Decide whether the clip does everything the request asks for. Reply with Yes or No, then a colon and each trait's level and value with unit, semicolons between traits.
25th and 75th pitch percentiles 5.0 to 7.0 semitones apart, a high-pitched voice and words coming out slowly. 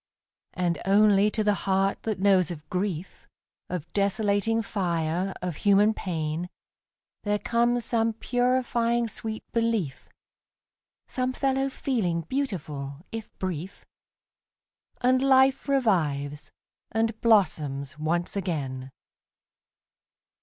Yes: average, 5.3 semitones; high, 200 Hz; slow, 100 wpm